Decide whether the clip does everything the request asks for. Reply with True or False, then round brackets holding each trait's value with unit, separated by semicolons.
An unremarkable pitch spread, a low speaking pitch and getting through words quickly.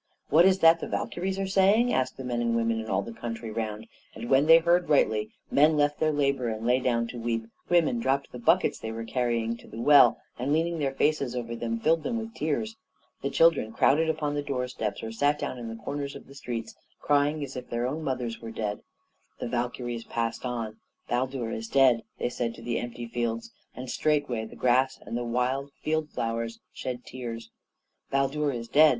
True (4.1 semitones; 125 Hz; 210 wpm)